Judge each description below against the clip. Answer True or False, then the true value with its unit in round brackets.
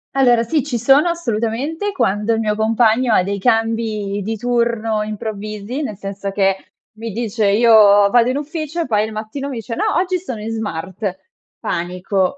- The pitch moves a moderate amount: True (3.2 semitones)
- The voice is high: True (225 Hz)